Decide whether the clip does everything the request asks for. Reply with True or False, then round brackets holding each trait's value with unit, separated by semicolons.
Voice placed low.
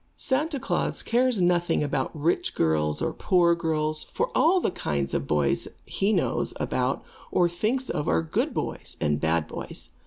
False (170 Hz)